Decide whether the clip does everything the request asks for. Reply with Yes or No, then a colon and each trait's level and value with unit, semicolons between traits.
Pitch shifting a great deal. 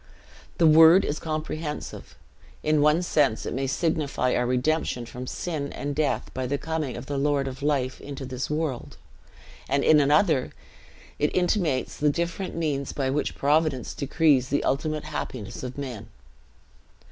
No: average, 2.9 semitones